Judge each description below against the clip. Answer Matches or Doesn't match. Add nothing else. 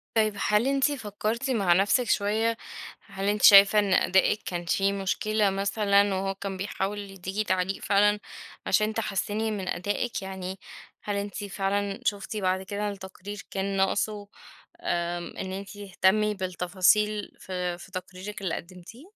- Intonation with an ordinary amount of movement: Doesn't match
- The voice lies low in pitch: Doesn't match